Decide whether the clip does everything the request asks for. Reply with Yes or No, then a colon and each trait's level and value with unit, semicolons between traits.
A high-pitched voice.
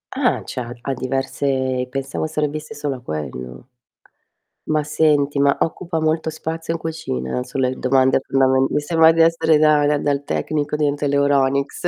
No: medium, 145 Hz